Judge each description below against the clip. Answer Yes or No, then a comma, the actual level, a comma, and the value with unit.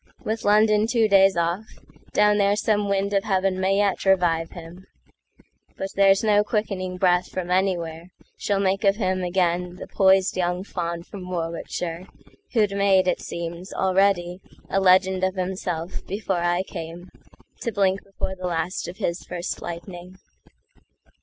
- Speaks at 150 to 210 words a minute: No, slow, 135 wpm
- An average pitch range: No, narrow, 2.0 semitones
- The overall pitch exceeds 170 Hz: Yes, medium, 185 Hz